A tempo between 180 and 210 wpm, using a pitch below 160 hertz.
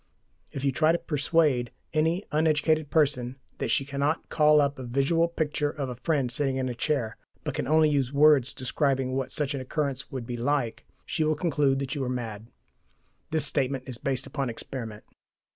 Yes: average, 190 wpm; medium, 140 Hz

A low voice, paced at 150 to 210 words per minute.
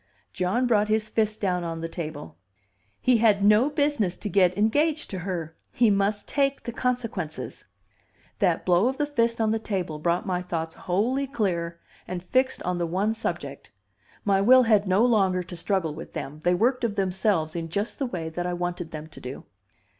No: high, 195 Hz; average, 190 wpm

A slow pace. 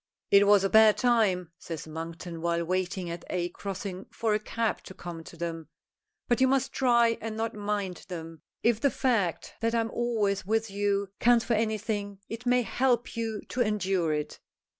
No: average, 185 wpm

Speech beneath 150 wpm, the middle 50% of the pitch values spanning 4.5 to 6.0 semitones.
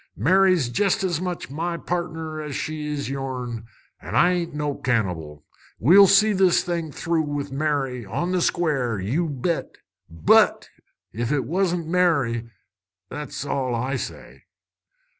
Yes: average, 140 wpm; wide, 5.5 semitones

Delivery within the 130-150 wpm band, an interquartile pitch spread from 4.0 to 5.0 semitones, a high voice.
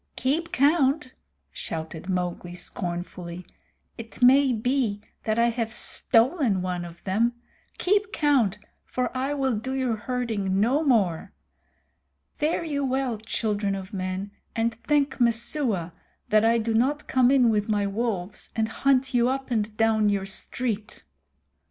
Yes: average, 140 wpm; average, 4.7 semitones; high, 230 Hz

